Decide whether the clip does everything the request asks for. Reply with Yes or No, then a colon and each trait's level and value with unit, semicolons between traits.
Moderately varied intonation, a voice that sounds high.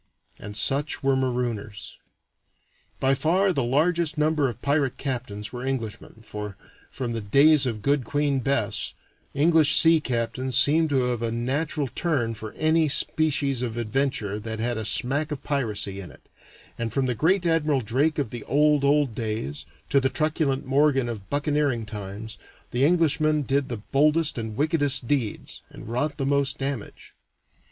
No: average, 4.4 semitones; low, 135 Hz